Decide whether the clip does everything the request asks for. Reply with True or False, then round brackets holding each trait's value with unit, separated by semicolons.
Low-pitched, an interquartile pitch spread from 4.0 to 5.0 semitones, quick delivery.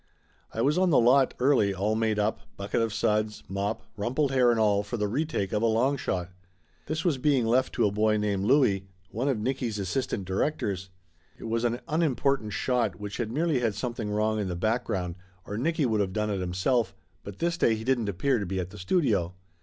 True (110 Hz; 4.3 semitones; 215 wpm)